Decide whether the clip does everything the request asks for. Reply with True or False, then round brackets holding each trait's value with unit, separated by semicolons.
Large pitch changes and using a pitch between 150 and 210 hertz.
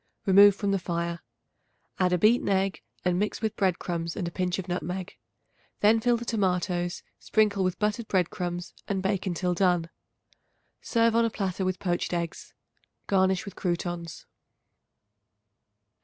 False (2.4 semitones; 185 Hz)